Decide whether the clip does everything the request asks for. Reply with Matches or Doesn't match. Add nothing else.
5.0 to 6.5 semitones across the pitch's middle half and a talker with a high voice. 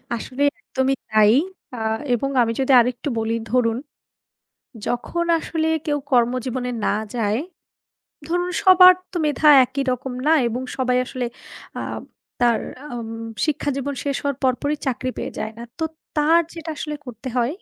Doesn't match